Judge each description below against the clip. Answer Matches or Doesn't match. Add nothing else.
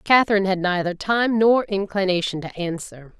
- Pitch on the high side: Matches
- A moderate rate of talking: Matches